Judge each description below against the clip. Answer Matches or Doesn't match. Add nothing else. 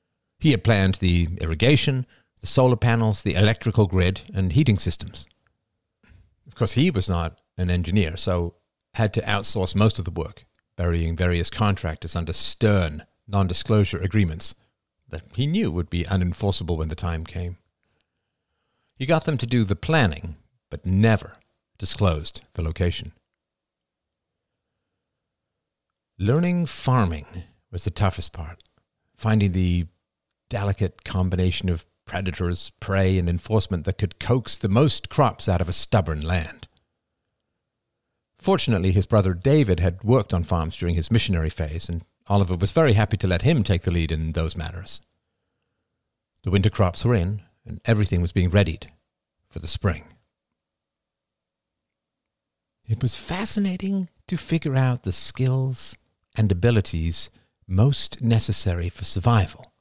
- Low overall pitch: Matches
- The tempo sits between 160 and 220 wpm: Doesn't match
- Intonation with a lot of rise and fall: Doesn't match